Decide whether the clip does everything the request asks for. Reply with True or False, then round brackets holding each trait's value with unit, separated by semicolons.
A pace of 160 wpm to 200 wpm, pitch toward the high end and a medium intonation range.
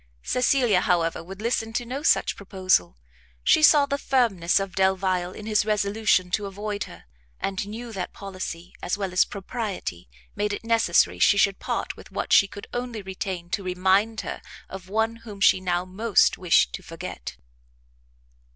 True (170 wpm; 195 Hz; 3.3 semitones)